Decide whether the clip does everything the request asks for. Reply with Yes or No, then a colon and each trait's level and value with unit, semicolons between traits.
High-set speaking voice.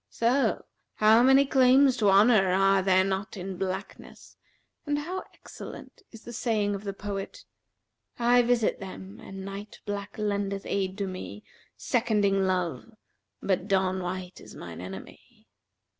Yes: high, 200 Hz